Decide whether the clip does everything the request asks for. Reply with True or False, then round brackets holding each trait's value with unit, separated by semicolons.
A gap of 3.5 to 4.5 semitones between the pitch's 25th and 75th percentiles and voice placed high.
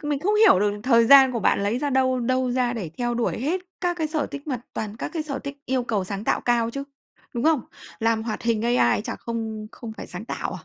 True (3.8 semitones; 240 Hz)